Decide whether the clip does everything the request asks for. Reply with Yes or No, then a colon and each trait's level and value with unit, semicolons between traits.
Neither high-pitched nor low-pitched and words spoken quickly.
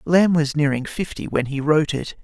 Yes: medium, 150 Hz; fast, 215 wpm